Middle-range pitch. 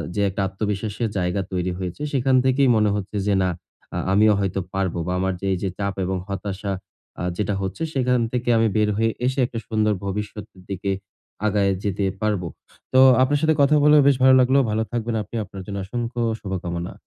No: low, 105 Hz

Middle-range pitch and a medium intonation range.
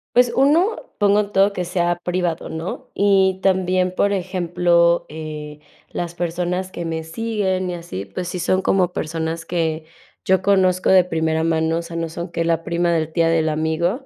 No: medium, 175 Hz; narrow, 2.3 semitones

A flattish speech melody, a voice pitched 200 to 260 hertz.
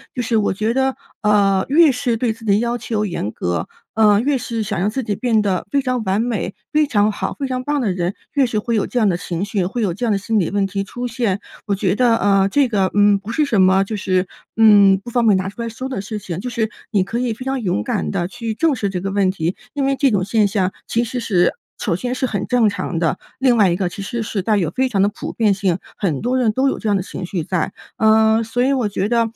No: average, 3.8 semitones; high, 215 Hz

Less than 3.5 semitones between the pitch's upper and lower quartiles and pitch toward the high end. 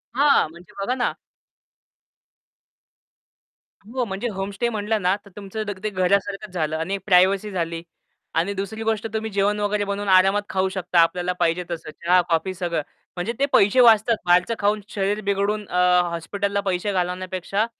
Yes: narrow, 2.6 semitones; high, 195 Hz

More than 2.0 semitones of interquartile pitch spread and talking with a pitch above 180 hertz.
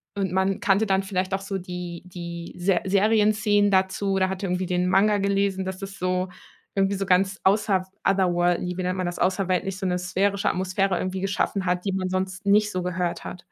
No: narrow, 1.4 semitones; high, 190 Hz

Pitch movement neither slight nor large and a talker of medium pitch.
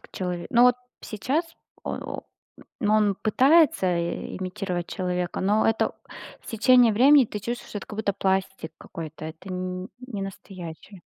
No: average, 3.6 semitones; high, 195 Hz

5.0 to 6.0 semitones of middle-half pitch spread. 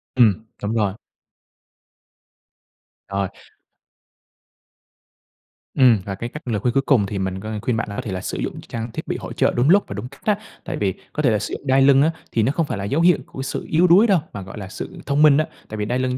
Yes: wide, 5.4 semitones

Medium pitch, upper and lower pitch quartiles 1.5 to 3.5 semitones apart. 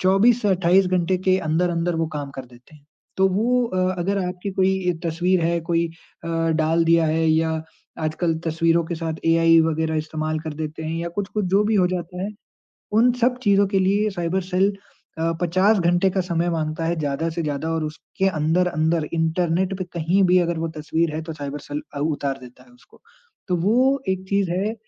Yes: medium, 170 Hz; average, 2.8 semitones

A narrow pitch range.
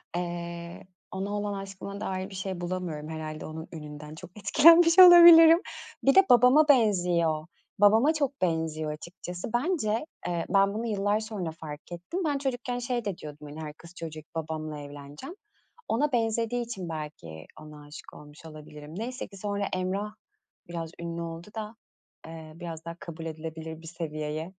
No: wide, 5.6 semitones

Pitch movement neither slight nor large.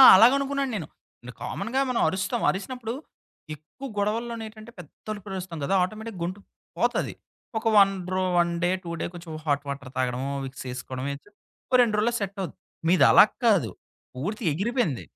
No: wide, 5.9 semitones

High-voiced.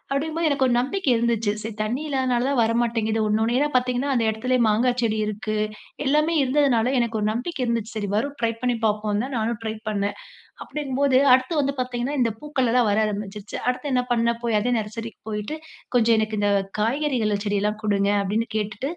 Yes: high, 235 Hz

